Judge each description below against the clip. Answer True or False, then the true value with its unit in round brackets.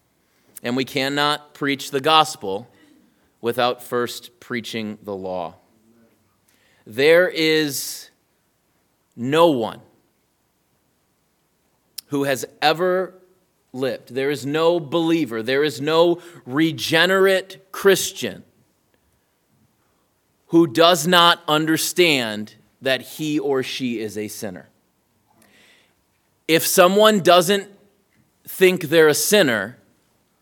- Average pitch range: False (5.9 semitones)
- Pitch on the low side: False (150 Hz)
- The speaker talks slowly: True (90 wpm)